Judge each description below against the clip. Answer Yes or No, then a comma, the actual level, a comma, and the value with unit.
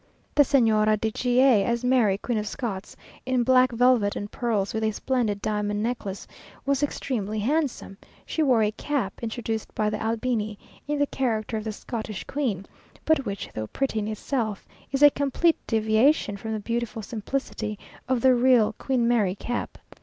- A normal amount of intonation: Yes, average, 3.3 semitones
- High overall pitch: Yes, high, 230 Hz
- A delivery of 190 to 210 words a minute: No, average, 175 wpm